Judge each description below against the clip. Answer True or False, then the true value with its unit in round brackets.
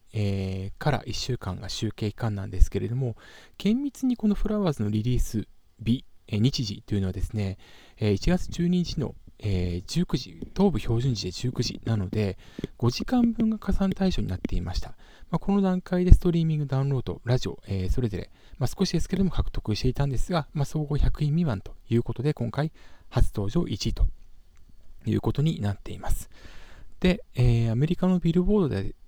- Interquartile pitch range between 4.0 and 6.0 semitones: False (8.7 semitones)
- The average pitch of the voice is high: False (115 Hz)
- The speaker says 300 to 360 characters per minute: True (325 characters per minute)